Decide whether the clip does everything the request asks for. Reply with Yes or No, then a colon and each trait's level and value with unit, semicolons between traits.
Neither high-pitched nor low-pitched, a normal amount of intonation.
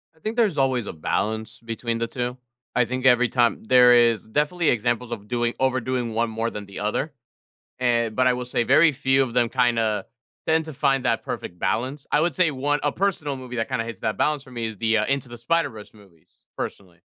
No: low, 125 Hz; average, 3.0 semitones